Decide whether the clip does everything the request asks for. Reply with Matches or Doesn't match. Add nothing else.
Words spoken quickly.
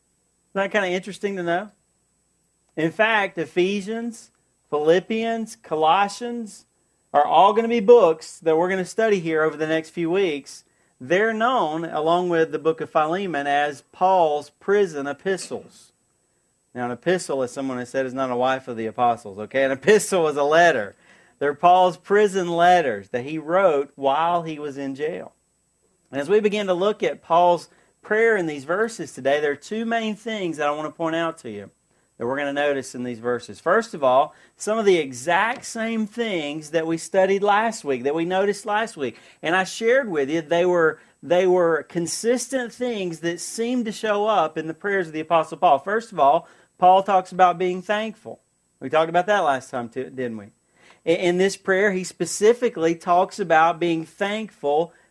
Doesn't match